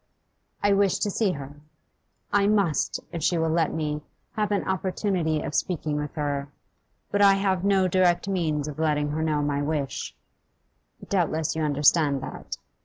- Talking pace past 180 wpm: No, average, 165 wpm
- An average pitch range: Yes, average, 4.3 semitones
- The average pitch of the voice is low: No, medium, 160 Hz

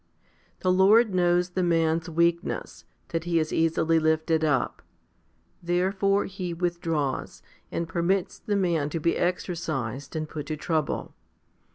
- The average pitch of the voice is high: No, medium, 170 Hz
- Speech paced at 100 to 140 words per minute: Yes, slow, 135 wpm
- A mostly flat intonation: Yes, narrow, 2.2 semitones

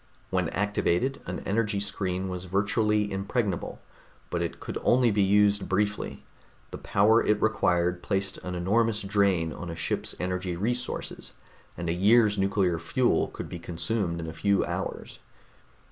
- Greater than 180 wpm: No, average, 150 wpm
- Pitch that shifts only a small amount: No, average, 3.0 semitones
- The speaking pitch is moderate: No, low, 100 Hz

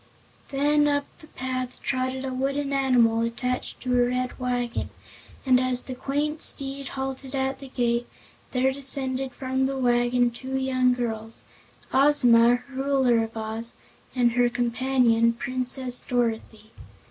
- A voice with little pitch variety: Yes, narrow, 1.7 semitones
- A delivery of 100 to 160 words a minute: Yes, slow, 135 wpm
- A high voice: Yes, very high, 255 Hz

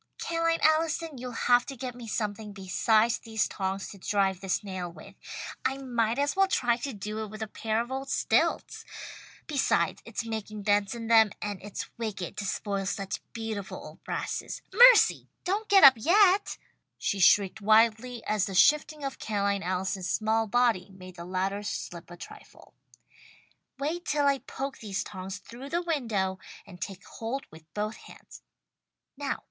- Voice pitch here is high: Yes, high, 220 Hz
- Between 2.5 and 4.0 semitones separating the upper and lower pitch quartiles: No, average, 5.3 semitones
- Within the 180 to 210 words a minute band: No, average, 165 wpm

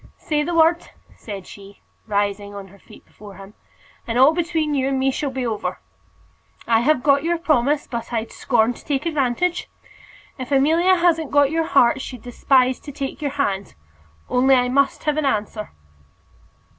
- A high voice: Yes, very high, 270 Hz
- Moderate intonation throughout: Yes, average, 4.8 semitones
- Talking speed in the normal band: Yes, average, 175 wpm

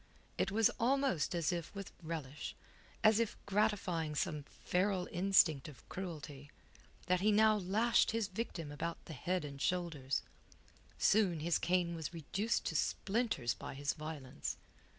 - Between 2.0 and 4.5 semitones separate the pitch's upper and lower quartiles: No, average, 5.1 semitones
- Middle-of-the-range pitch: Yes, medium, 175 Hz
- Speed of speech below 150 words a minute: Yes, average, 140 wpm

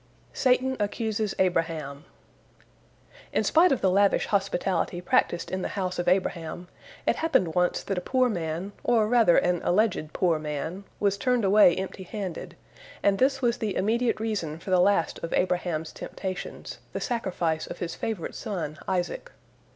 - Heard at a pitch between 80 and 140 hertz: No, high, 190 Hz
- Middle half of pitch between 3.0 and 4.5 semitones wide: Yes, average, 3.9 semitones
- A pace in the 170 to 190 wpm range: No, average, 160 wpm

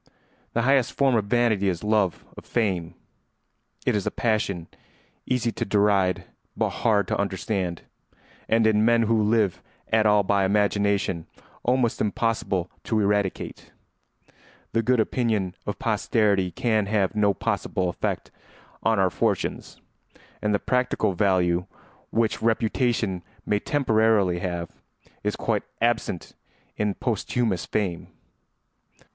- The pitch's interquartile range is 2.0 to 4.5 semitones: Yes, average, 3.0 semitones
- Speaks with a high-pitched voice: No, low, 105 Hz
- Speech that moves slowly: Yes, slow, 130 wpm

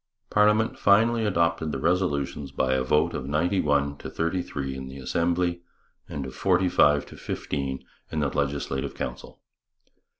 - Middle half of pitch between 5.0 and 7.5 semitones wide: No, average, 4.4 semitones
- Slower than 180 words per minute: Yes, average, 160 wpm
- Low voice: Yes, very low, 75 Hz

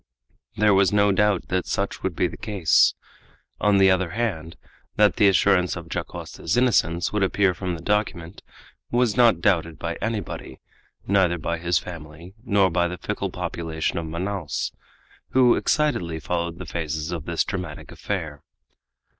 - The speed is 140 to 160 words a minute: Yes, average, 155 wpm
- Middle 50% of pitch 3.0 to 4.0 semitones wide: Yes, average, 3.5 semitones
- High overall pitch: No, very low, 90 Hz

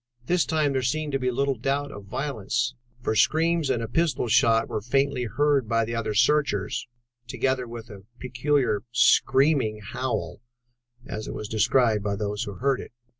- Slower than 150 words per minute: No, average, 170 wpm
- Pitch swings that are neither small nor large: Yes, average, 4.3 semitones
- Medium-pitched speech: No, low, 125 Hz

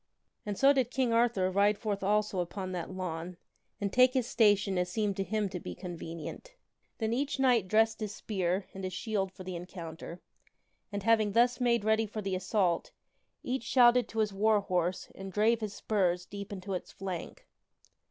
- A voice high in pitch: Yes, high, 205 Hz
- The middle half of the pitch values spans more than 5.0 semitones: No, average, 3.3 semitones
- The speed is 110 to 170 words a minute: No, average, 185 wpm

